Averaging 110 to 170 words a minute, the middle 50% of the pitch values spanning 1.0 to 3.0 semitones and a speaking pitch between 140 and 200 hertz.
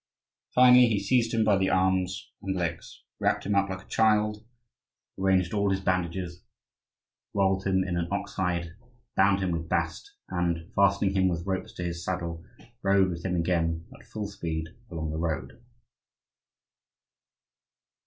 No: average, 155 wpm; narrow, 2.4 semitones; very low, 95 Hz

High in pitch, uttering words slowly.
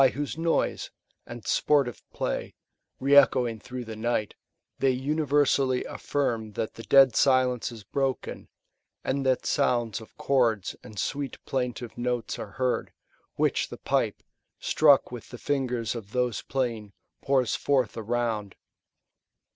No: low, 125 Hz; slow, 130 wpm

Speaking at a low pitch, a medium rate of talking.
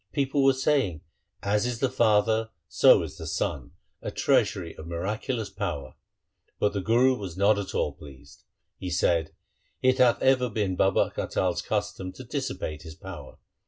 Yes: low, 105 Hz; average, 170 wpm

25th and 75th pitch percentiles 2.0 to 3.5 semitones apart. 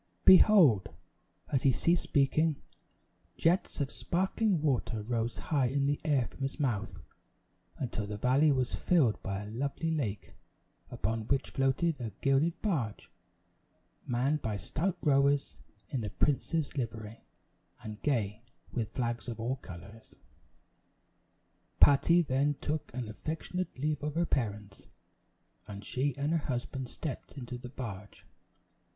No: average, 4.9 semitones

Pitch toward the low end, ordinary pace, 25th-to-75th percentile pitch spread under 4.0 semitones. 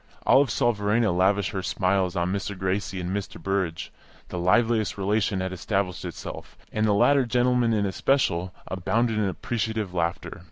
Yes: low, 100 Hz; average, 160 wpm; average, 3.3 semitones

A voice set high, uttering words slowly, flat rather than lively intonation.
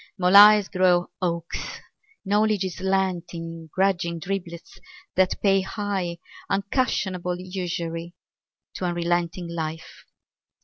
No: medium, 180 Hz; slow, 100 wpm; narrow, 2.2 semitones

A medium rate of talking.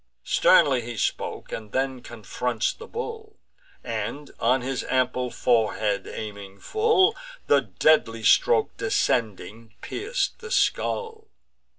No: slow, 110 wpm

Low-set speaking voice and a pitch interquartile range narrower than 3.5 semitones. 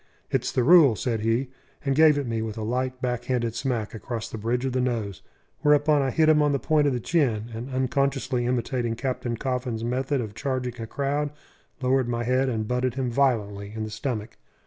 Yes: low, 125 Hz; average, 2.9 semitones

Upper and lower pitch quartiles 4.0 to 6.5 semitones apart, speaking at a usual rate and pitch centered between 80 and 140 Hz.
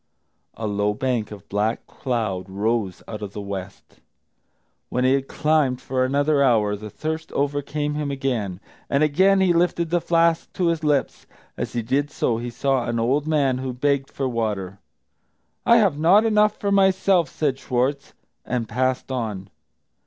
Yes: wide, 5.4 semitones; average, 165 wpm; low, 135 Hz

